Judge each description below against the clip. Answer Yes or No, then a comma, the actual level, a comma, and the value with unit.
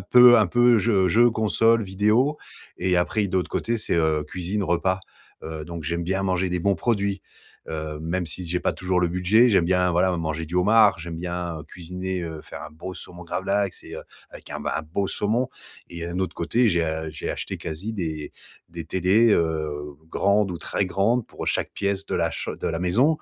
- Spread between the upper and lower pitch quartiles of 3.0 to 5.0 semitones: Yes, average, 3.4 semitones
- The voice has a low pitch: Yes, very low, 90 Hz